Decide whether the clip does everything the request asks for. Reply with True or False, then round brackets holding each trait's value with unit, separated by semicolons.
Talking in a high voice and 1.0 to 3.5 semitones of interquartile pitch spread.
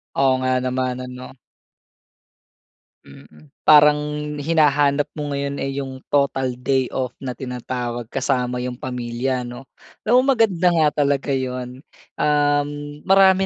False (135 Hz; 2.6 semitones)